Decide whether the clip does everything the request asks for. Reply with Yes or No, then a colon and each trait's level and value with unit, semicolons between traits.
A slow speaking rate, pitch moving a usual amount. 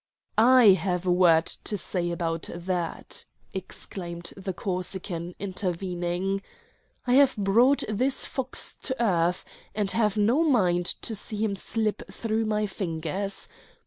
Yes: slow, 130 wpm; average, 3.8 semitones